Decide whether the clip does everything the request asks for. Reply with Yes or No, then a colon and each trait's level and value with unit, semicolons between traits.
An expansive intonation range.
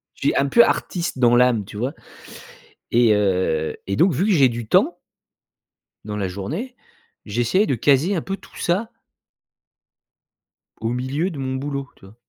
Yes: wide, 7.3 semitones